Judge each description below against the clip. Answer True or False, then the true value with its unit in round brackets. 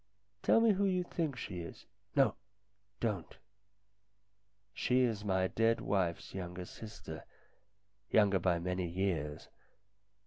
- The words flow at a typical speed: False (115 wpm)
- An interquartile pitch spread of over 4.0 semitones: True (4.5 semitones)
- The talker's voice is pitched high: False (95 Hz)